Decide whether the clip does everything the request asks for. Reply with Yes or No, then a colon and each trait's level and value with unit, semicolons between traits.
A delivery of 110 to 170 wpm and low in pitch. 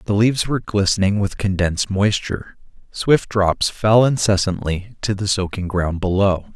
Yes: average, 145 wpm; low, 100 Hz